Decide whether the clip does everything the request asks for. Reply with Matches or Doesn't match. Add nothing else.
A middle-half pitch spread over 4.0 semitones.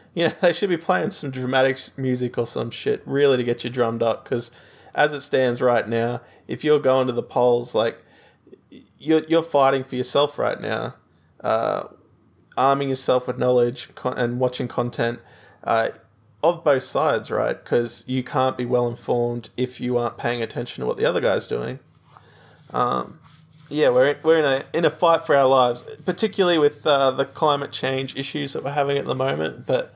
Doesn't match